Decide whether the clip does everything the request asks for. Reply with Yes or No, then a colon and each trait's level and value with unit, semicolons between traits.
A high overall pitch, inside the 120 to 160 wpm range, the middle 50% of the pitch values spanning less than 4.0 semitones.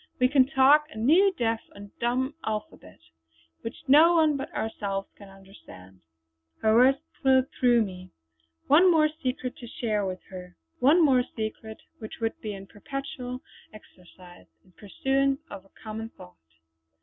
No: high, 230 Hz; average, 150 wpm; average, 5.2 semitones